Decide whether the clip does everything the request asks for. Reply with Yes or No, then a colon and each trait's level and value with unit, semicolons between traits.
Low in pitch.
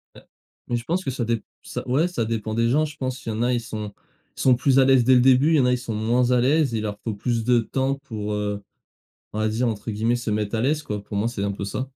Yes: low, 120 Hz